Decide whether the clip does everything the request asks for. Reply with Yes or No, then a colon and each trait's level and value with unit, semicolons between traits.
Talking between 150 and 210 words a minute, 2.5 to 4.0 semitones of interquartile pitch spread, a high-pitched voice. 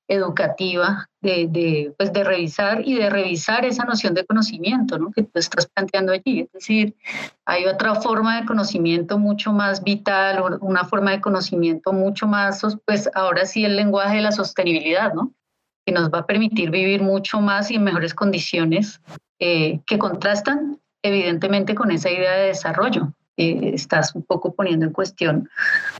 Yes: average, 165 wpm; average, 2.9 semitones; high, 195 Hz